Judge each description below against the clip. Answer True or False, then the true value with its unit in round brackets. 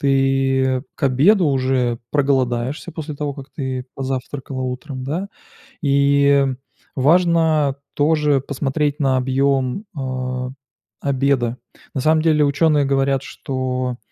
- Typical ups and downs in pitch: False (2.1 semitones)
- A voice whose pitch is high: False (135 Hz)